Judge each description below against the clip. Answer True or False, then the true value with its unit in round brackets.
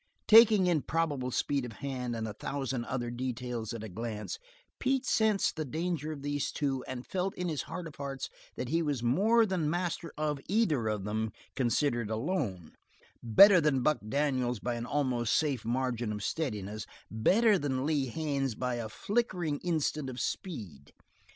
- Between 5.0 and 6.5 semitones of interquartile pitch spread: True (5.5 semitones)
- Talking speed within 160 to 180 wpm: True (170 wpm)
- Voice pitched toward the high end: False (135 Hz)